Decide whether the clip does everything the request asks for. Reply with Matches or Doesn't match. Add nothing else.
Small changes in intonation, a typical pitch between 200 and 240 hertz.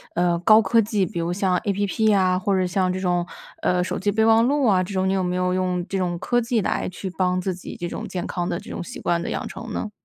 Doesn't match